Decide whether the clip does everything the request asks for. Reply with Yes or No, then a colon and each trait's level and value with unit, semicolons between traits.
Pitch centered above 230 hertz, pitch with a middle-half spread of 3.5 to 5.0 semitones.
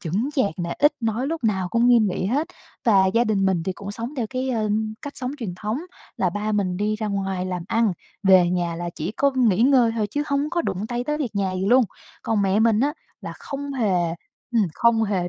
No: high, 215 Hz; average, 4.6 semitones